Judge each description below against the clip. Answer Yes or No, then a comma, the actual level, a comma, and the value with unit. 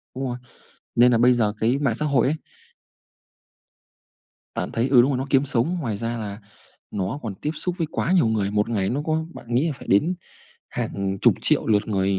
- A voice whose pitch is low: Yes, low, 120 Hz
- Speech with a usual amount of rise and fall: Yes, average, 4.8 semitones